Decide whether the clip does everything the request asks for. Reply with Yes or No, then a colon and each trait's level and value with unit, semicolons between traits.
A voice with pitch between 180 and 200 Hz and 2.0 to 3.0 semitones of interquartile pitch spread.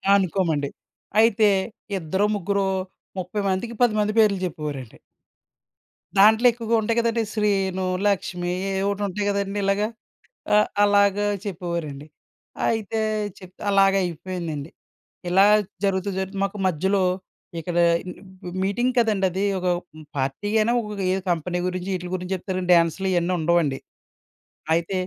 Yes: high, 190 Hz; narrow, 2.6 semitones